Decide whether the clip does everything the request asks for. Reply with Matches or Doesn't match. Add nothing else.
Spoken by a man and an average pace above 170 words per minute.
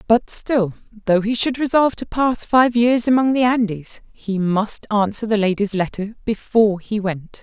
Doesn't match